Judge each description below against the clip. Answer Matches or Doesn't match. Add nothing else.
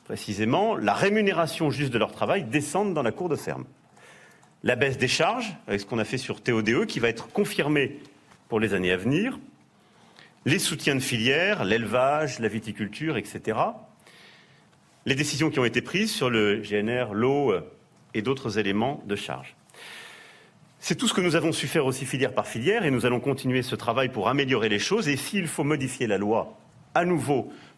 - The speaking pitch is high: Doesn't match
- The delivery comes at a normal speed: Matches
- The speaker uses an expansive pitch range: Matches